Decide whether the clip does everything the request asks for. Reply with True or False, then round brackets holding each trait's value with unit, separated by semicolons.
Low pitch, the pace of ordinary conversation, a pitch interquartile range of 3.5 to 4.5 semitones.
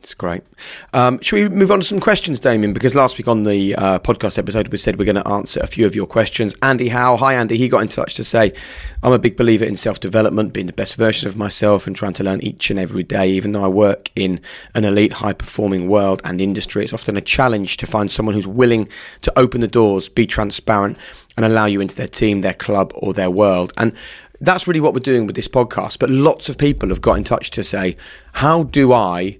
False (110 Hz; 245 wpm; 4.0 semitones)